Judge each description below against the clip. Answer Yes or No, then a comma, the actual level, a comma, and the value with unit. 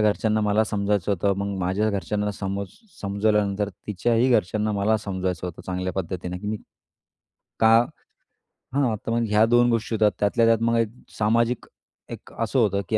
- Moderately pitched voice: No, low, 105 Hz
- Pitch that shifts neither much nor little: No, narrow, 2.0 semitones